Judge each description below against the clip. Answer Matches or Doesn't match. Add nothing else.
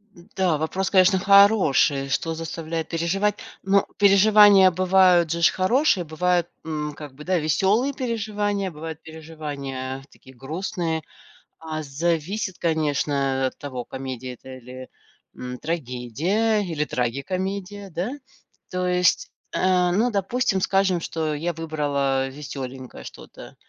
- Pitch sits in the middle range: Matches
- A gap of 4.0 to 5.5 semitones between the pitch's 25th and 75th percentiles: Matches